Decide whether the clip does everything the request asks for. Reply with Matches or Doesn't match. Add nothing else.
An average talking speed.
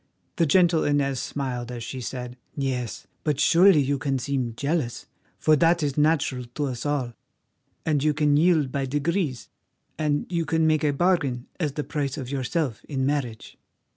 Matches